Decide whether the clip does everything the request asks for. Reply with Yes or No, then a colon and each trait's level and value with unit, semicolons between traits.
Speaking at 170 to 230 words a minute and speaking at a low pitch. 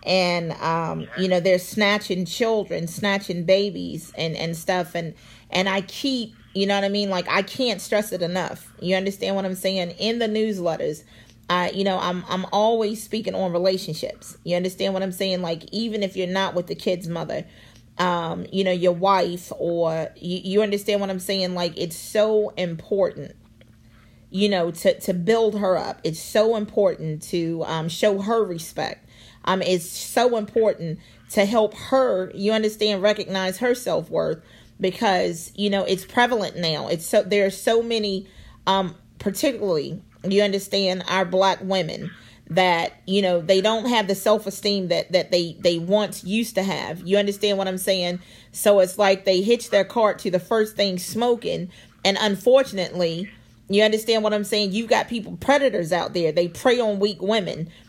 No: average, 175 wpm; high, 190 Hz